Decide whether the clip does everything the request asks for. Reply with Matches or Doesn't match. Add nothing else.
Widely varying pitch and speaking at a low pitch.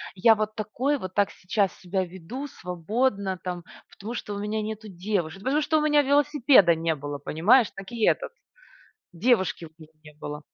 Doesn't match